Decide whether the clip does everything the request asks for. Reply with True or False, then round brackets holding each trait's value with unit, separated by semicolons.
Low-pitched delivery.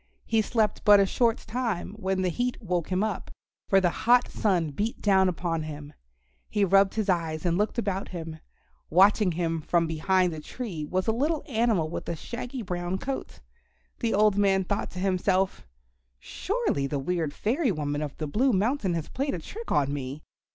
False (190 Hz)